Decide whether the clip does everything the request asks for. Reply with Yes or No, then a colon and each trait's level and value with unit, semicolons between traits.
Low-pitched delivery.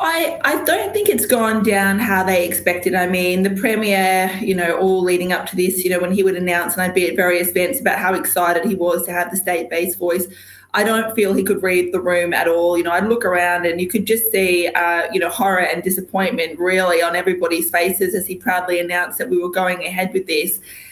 No: medium, 185 Hz